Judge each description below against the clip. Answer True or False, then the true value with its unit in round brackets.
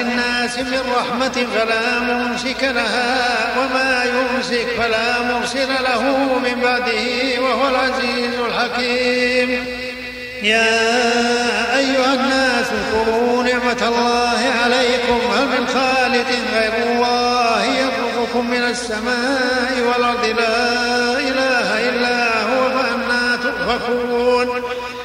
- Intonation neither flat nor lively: False (0.7 semitones)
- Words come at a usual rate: True (90 wpm)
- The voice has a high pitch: True (245 Hz)